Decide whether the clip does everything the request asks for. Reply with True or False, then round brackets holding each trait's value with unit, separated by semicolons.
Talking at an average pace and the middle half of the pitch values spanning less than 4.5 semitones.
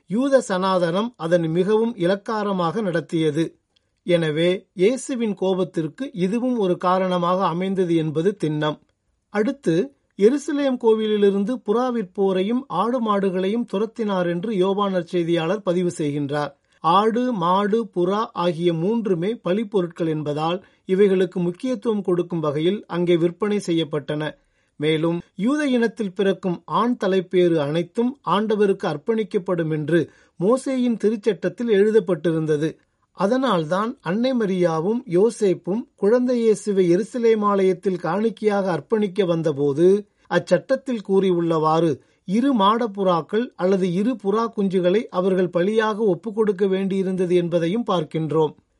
True (95 wpm; 4.1 semitones)